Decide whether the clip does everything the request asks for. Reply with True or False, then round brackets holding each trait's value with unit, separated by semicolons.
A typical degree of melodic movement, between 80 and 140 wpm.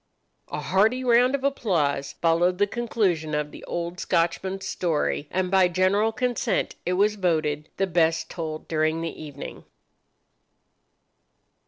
True (4.2 semitones; 135 wpm)